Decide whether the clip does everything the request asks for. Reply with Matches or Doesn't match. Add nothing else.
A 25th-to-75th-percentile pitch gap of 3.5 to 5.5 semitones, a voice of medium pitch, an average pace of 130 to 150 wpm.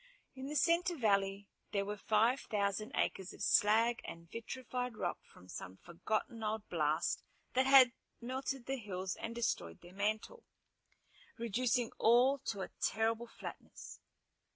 Doesn't match